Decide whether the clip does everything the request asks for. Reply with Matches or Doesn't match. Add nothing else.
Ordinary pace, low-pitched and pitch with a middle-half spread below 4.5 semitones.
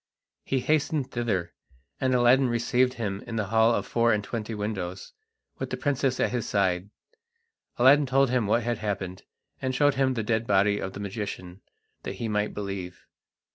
Matches